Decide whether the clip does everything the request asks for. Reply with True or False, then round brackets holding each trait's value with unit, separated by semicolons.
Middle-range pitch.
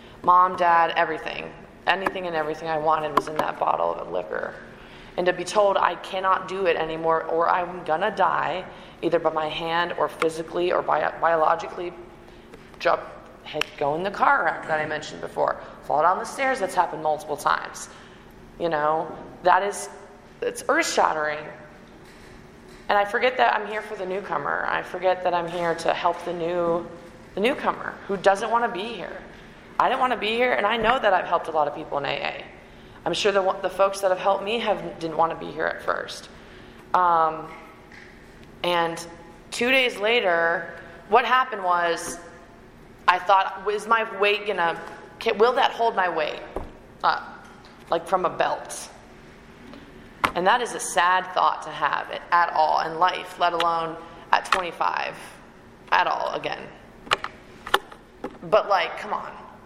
True (175 Hz)